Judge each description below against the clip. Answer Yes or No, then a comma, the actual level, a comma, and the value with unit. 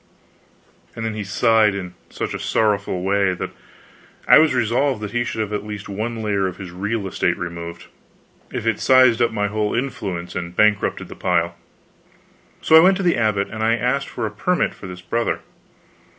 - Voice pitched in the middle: No, low, 105 Hz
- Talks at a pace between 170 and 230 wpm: Yes, average, 185 wpm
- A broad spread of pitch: No, average, 3.4 semitones